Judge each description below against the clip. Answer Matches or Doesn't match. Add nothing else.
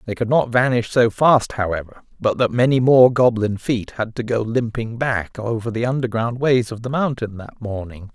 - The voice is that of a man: Matches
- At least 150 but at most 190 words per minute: Doesn't match